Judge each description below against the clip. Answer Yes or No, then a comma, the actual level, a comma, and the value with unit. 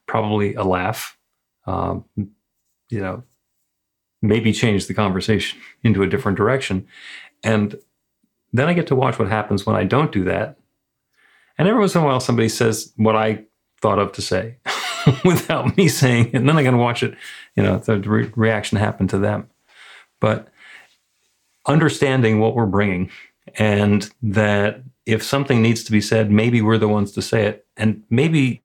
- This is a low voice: Yes, low, 110 Hz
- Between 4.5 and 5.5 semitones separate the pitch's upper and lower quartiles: No, average, 3.4 semitones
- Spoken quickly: No, average, 170 wpm